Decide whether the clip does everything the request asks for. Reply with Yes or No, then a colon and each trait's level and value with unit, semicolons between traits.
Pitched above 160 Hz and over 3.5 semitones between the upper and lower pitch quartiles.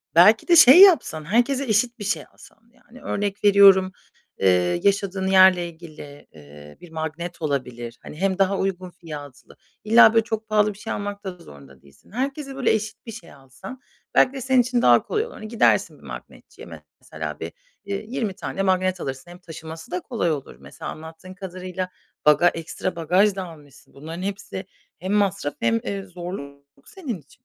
Yes: medium, 185 Hz; average, 5.1 semitones